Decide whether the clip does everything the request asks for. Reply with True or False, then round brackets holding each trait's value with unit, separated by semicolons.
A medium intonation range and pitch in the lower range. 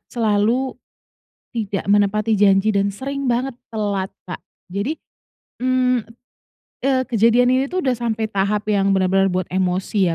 False (4.1 semitones; 215 Hz)